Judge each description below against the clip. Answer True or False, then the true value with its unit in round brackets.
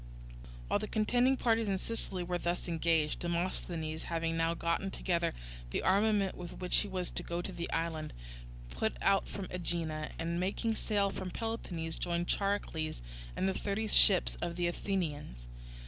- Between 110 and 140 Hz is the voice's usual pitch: False (175 Hz)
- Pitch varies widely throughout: False (3.1 semitones)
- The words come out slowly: False (165 wpm)